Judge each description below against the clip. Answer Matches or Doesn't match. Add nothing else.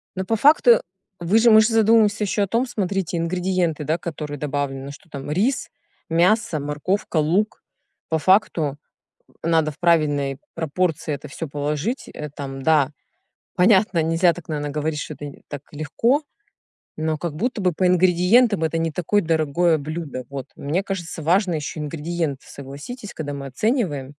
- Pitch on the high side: Doesn't match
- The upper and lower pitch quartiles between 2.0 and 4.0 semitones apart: Doesn't match